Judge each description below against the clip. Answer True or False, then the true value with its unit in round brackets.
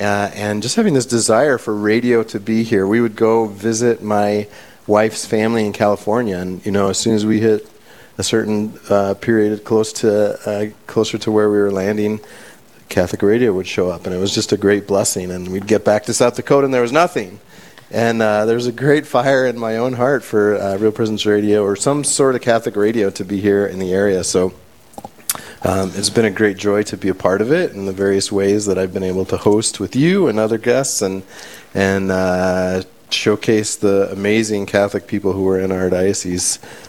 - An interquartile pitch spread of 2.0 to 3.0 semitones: True (2.4 semitones)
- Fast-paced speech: True (220 wpm)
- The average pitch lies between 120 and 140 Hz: False (105 Hz)